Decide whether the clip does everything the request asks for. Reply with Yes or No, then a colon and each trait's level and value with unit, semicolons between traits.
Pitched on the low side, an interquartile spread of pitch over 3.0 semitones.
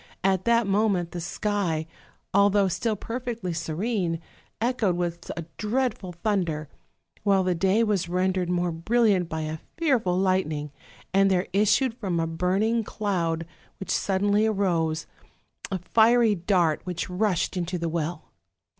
No: high, 190 Hz; average, 3.7 semitones